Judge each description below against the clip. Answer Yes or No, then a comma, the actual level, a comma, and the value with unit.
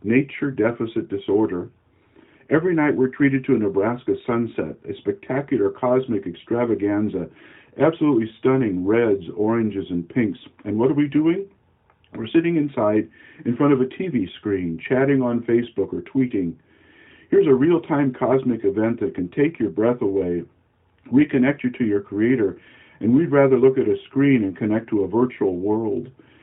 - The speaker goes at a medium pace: Yes, average, 160 wpm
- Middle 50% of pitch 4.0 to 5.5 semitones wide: Yes, average, 4.6 semitones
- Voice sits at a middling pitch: No, low, 120 Hz